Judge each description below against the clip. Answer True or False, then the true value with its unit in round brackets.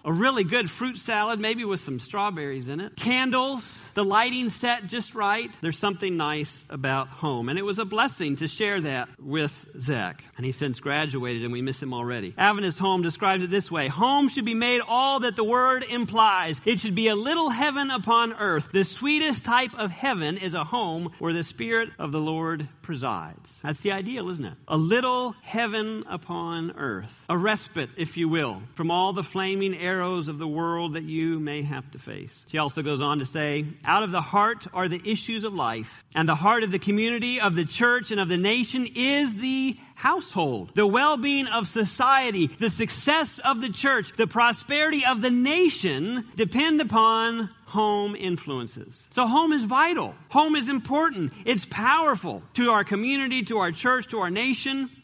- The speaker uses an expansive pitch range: True (7.3 semitones)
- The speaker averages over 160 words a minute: True (190 wpm)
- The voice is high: True (205 Hz)